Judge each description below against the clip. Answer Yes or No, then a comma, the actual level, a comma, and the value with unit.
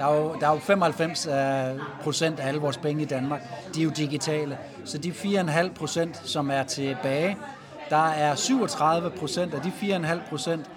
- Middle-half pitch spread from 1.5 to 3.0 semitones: Yes, narrow, 2.5 semitones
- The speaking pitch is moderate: Yes, medium, 155 Hz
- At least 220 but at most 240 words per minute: No, average, 185 wpm